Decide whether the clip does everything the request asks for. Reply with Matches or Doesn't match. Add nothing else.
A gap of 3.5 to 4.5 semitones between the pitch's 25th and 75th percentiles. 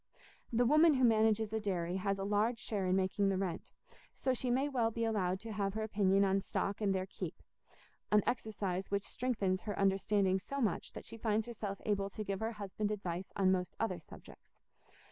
Doesn't match